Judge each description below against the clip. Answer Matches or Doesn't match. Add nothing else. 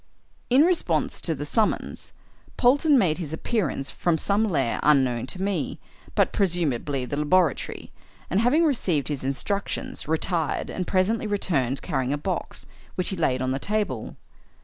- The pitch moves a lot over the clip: Matches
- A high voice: Doesn't match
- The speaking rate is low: Doesn't match